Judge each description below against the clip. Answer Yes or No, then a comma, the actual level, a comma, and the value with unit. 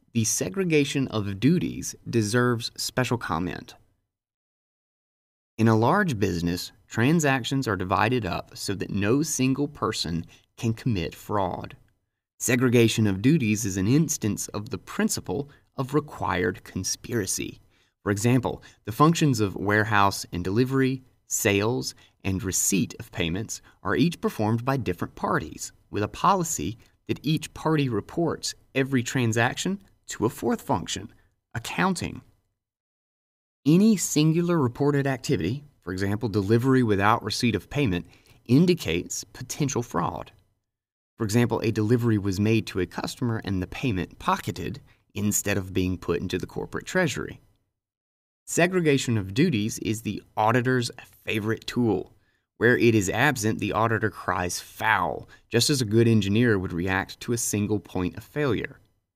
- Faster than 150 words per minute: No, slow, 135 wpm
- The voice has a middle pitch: No, low, 115 Hz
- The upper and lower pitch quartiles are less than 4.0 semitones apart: No, average, 4.8 semitones